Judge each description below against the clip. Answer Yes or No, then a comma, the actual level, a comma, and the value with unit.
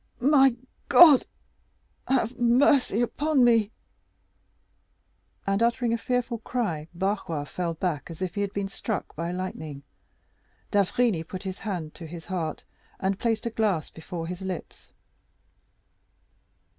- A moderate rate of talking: No, slow, 130 wpm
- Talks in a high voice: Yes, high, 195 Hz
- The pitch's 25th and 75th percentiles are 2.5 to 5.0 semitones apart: No, wide, 5.5 semitones